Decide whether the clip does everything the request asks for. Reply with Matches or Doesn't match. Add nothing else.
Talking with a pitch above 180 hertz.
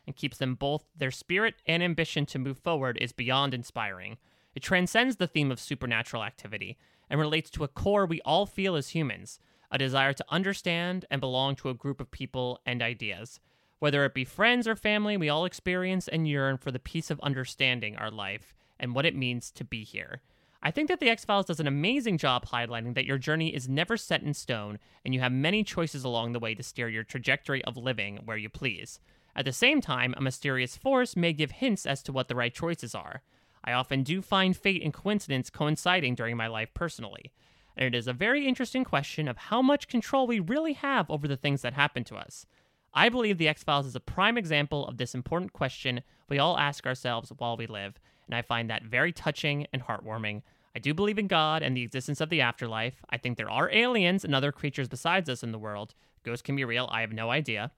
Doesn't match